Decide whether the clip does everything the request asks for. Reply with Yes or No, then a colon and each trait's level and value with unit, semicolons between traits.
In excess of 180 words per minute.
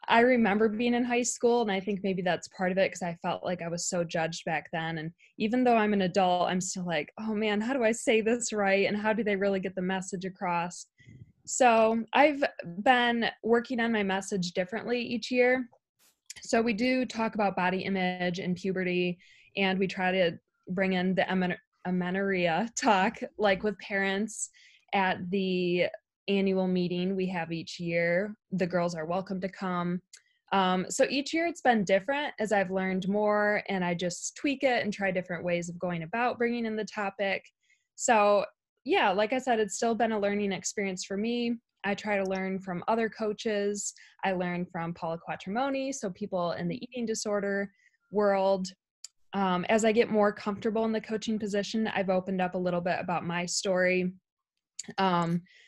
Yes: average, 190 wpm